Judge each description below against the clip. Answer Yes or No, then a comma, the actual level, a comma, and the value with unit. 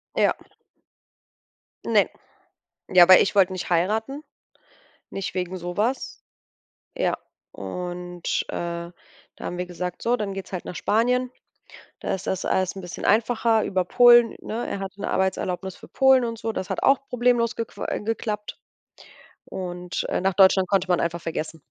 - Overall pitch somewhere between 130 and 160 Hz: No, high, 190 Hz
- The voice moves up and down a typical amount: Yes, average, 4.2 semitones